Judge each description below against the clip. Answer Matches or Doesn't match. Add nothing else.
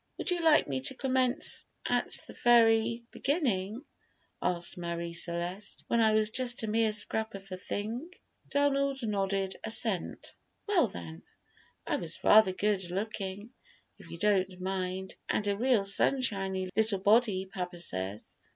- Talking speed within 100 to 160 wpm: Matches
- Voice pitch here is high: Matches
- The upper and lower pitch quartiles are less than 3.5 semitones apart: Doesn't match